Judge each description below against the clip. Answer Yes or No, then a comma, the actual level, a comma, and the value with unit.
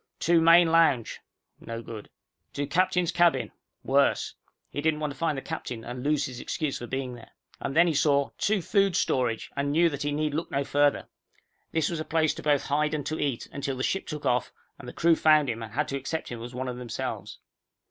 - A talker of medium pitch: Yes, medium, 145 Hz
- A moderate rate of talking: No, fast, 225 wpm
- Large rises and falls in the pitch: No, average, 3.8 semitones